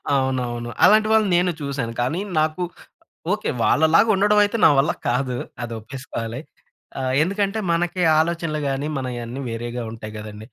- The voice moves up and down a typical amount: No, wide, 6.9 semitones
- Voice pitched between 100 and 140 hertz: Yes, low, 135 Hz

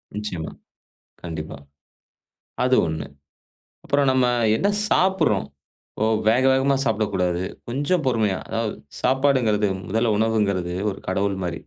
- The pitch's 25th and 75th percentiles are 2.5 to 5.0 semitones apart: No, wide, 5.6 semitones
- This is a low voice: Yes, low, 110 Hz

